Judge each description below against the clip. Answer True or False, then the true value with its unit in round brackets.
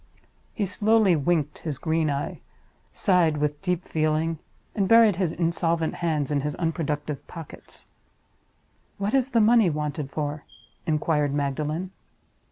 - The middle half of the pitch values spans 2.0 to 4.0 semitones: True (3.5 semitones)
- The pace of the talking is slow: True (130 wpm)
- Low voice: False (160 Hz)